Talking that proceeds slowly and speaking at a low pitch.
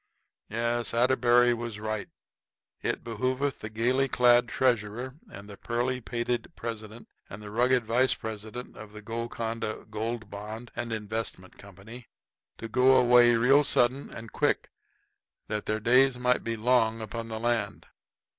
No: average, 145 wpm; low, 115 Hz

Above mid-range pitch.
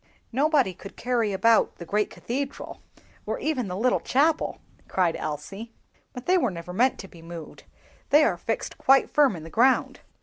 Yes: high, 230 Hz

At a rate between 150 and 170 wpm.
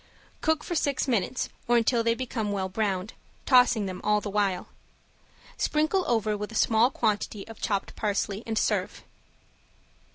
Yes: average, 155 wpm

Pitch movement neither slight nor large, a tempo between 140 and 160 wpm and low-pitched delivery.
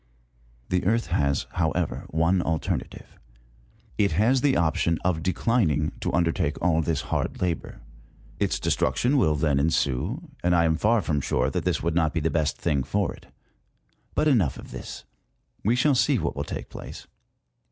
No: average, 4.6 semitones; average, 175 wpm; very low, 85 Hz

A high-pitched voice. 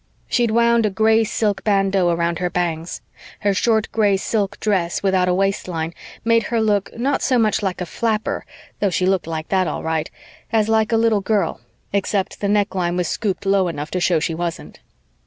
Yes: high, 195 Hz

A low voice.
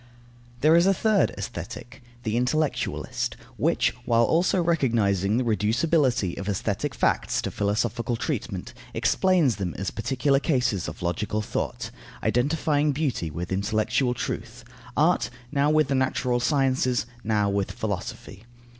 Yes: low, 120 Hz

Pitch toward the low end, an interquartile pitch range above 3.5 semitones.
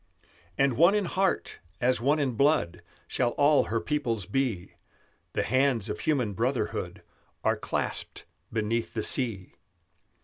Yes: low, 125 Hz; average, 4.7 semitones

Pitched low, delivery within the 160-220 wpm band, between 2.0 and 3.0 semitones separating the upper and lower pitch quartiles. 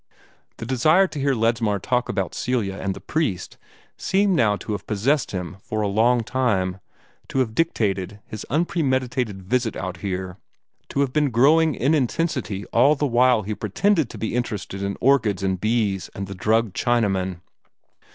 No: low, 115 Hz; average, 170 wpm; average, 5.1 semitones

